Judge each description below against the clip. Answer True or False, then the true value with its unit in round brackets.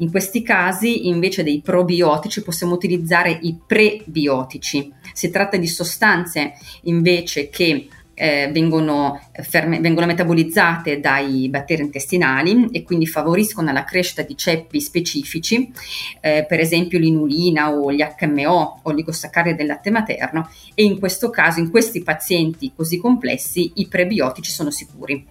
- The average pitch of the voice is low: False (170 Hz)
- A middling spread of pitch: True (3.1 semitones)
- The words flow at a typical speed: True (135 wpm)